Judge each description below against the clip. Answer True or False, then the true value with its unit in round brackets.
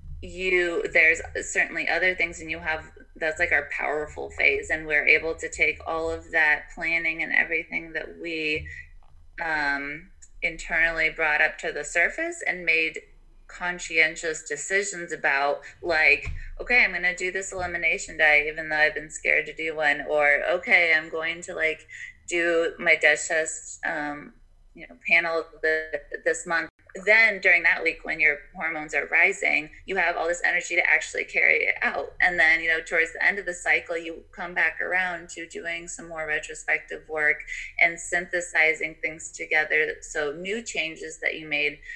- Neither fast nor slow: True (175 wpm)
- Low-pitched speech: False (165 Hz)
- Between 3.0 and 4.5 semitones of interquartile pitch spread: False (2.6 semitones)